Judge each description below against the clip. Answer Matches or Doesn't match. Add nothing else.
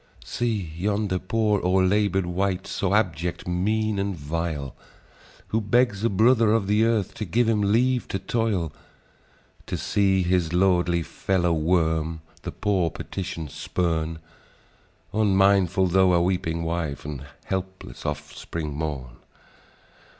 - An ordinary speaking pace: Doesn't match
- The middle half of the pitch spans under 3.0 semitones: Doesn't match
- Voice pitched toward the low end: Matches